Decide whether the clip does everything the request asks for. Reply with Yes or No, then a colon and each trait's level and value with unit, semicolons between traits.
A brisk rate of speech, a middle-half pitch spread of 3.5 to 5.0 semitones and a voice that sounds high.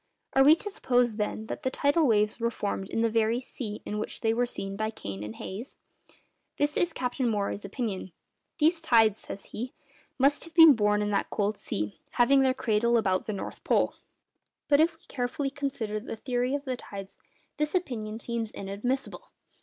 No: average, 185 wpm; average, 4.5 semitones; high, 235 Hz